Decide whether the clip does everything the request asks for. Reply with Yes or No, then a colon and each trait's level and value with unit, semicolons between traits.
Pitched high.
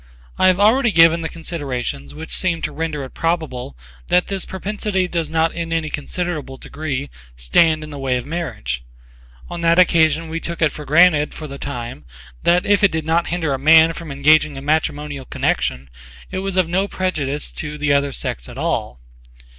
No: medium, 160 Hz